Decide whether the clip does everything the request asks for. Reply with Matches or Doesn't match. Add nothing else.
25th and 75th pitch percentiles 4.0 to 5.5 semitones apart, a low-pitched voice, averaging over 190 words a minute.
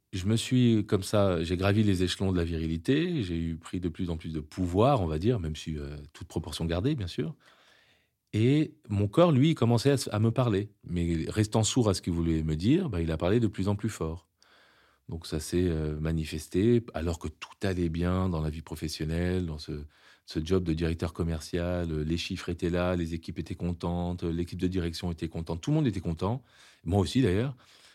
Matches